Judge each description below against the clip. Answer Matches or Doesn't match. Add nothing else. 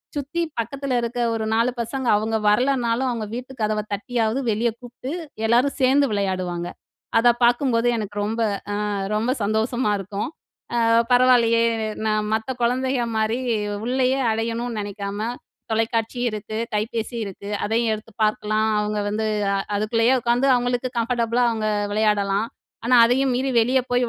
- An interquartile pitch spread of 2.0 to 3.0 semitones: Matches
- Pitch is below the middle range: Doesn't match